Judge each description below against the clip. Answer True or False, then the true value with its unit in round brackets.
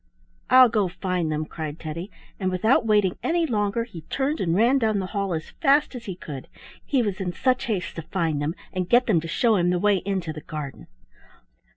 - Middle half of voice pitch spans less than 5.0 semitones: False (5.6 semitones)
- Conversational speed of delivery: False (215 wpm)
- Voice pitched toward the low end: False (190 Hz)